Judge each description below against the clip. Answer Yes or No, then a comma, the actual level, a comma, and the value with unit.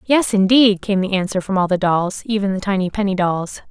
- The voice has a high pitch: Yes, high, 195 Hz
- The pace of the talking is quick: Yes, fast, 225 wpm